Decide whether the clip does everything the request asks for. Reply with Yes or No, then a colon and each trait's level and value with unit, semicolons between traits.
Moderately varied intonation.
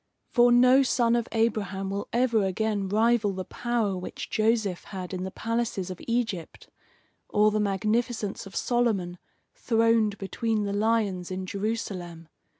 Yes: average, 3.2 semitones